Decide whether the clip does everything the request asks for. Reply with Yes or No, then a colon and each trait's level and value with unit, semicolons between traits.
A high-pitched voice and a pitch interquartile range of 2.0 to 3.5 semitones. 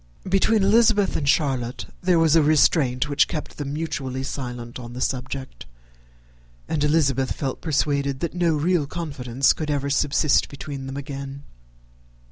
No: medium, 140 Hz; average, 3.2 semitones